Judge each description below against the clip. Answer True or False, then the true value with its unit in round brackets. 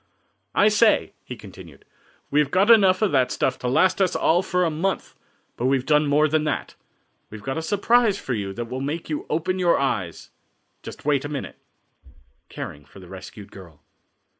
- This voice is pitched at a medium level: True (150 Hz)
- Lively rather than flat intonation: True (7.4 semitones)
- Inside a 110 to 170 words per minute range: False (195 wpm)